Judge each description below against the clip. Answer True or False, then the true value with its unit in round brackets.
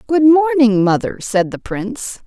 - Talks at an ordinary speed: True (160 wpm)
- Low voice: False (250 Hz)